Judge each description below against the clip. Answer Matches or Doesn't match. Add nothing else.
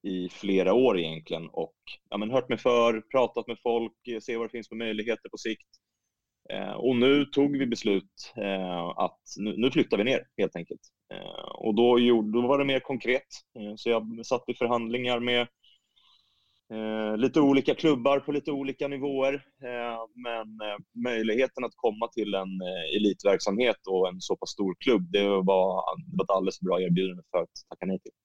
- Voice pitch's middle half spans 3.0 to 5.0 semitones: Matches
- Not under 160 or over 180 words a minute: Matches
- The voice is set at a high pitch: Doesn't match